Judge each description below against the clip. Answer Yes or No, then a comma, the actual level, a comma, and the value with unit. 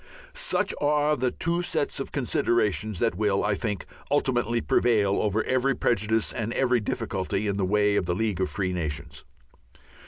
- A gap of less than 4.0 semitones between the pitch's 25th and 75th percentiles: No, average, 4.3 semitones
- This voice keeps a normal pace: Yes, average, 165 wpm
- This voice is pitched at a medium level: No, low, 110 Hz